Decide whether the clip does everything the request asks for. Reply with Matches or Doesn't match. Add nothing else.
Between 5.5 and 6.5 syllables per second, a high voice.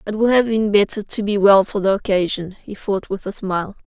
Matches